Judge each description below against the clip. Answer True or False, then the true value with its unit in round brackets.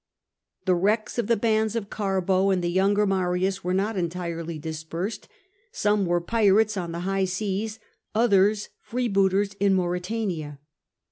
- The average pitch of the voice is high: True (195 Hz)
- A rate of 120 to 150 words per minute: True (140 wpm)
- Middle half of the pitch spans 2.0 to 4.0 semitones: True (2.8 semitones)